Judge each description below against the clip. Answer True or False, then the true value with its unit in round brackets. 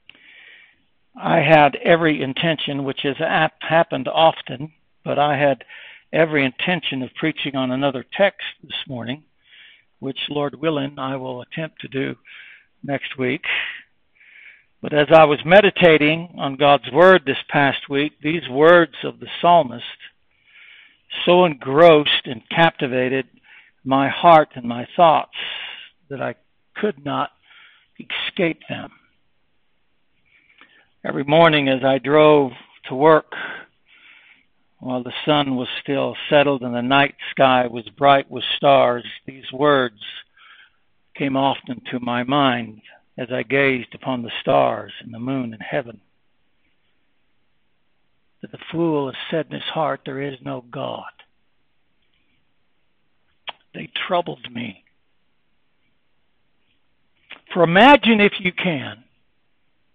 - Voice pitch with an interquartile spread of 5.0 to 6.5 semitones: False (3.5 semitones)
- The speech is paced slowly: True (120 wpm)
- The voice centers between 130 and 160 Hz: True (140 Hz)